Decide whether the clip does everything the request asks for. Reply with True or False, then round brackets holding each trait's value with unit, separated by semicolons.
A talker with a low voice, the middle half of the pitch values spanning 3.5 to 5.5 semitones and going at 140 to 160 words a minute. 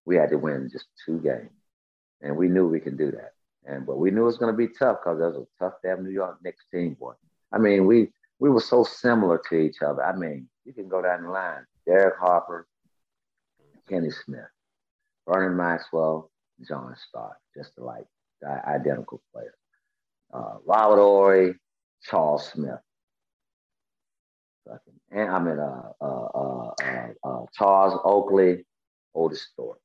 False (95 Hz; 4.0 semitones; 170 wpm)